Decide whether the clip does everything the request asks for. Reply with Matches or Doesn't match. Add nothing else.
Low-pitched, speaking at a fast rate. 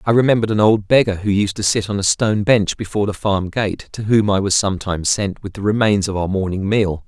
Matches